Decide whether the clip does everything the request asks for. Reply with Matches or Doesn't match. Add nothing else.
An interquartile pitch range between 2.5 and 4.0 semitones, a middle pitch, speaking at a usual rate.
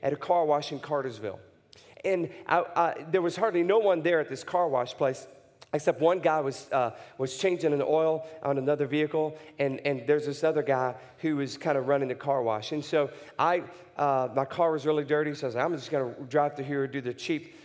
Doesn't match